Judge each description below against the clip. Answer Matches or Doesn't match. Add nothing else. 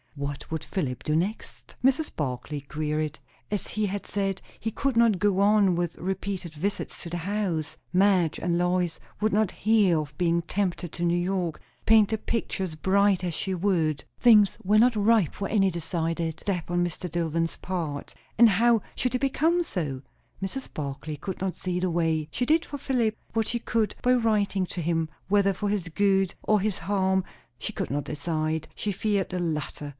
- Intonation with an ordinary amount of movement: Matches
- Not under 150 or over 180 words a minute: Doesn't match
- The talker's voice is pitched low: Doesn't match